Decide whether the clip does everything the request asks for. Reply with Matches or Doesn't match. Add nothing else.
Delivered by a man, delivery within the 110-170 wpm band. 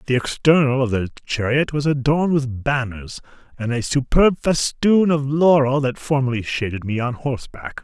Matches